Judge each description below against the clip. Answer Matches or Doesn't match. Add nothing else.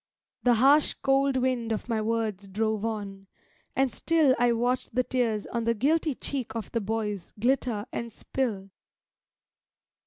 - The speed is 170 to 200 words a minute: Doesn't match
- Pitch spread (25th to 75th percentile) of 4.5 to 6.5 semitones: Doesn't match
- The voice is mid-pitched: Doesn't match